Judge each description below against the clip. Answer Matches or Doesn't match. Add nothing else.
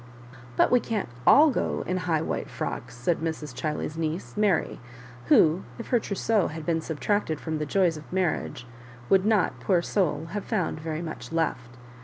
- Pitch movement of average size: Matches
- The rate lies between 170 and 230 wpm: Matches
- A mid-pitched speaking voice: Matches